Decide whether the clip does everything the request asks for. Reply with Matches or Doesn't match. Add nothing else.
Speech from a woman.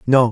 Doesn't match